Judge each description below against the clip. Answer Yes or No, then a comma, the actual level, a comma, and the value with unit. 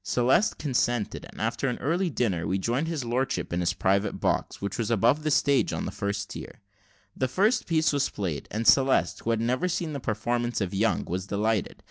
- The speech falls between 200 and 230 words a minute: Yes, fast, 205 wpm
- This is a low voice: Yes, low, 120 Hz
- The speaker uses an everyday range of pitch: No, wide, 5.7 semitones